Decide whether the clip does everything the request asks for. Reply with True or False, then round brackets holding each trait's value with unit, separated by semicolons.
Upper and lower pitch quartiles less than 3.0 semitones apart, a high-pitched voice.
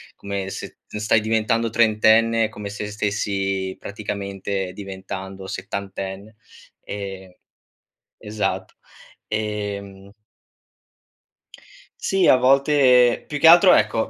False (2.6 semitones; 105 Hz)